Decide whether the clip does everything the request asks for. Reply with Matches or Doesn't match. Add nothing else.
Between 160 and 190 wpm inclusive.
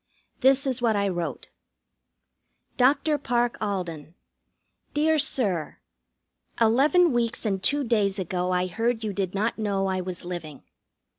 Doesn't match